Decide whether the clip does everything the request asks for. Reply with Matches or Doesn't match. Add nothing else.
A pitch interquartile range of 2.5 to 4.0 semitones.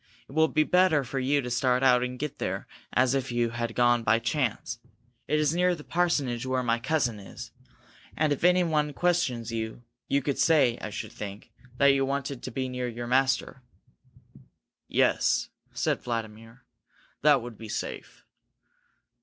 Matches